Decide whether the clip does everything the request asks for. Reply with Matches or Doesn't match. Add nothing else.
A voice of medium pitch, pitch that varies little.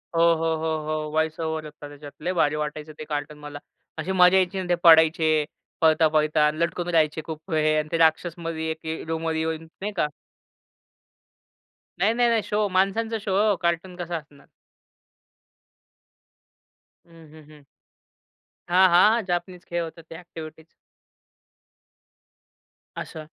Matches